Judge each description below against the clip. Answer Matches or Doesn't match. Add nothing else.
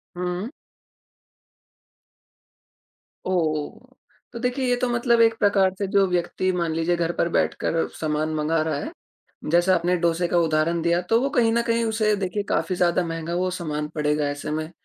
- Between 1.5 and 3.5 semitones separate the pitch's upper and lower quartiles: Doesn't match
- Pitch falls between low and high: Matches